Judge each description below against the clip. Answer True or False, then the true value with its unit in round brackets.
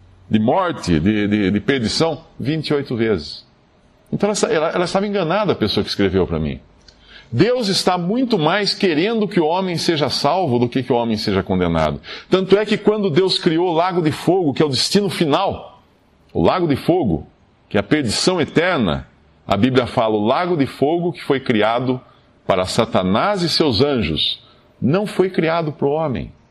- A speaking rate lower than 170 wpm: False (185 wpm)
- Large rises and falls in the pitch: True (8.7 semitones)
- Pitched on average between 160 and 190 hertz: False (150 Hz)